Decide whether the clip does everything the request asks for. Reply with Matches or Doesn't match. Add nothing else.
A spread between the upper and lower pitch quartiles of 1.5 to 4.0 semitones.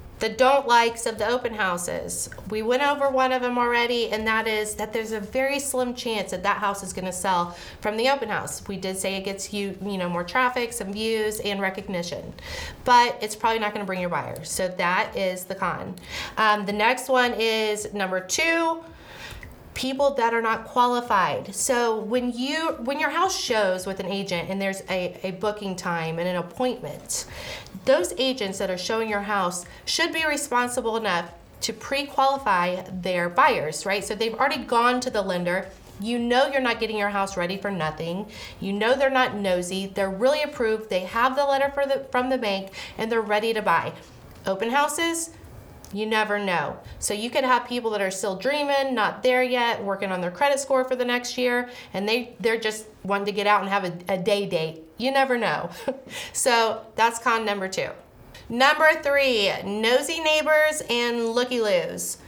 Doesn't match